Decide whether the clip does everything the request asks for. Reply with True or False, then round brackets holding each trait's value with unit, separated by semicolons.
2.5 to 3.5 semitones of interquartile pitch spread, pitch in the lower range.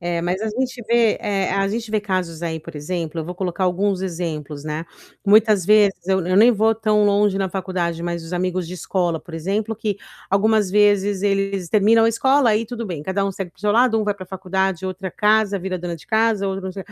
False (3.0 semitones; 195 Hz)